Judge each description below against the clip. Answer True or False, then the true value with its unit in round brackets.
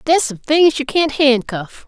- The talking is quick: False (190 wpm)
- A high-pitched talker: True (275 Hz)